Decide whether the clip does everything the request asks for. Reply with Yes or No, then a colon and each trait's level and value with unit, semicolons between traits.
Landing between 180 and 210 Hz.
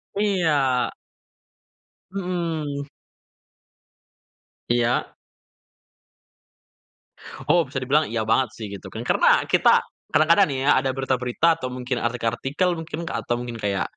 No: low, 135 Hz